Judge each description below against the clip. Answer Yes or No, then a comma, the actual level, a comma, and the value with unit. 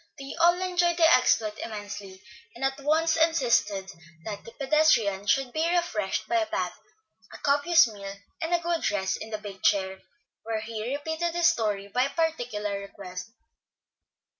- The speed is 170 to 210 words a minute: No, average, 160 wpm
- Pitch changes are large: Yes, wide, 7.9 semitones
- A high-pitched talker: Yes, high, 245 Hz